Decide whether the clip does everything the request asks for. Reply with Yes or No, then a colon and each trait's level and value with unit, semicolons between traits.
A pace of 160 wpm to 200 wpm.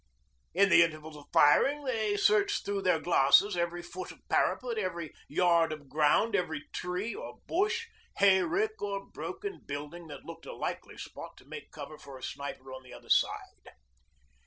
Yes: average, 170 wpm